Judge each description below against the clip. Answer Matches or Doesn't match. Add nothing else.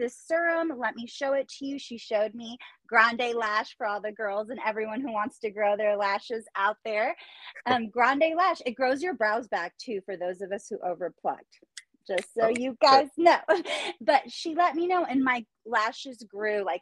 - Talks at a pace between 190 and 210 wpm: Matches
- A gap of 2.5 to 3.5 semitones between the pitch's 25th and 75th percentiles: Doesn't match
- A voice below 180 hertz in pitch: Doesn't match